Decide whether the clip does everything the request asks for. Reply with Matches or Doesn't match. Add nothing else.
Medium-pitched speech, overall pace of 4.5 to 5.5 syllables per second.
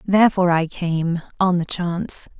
Matches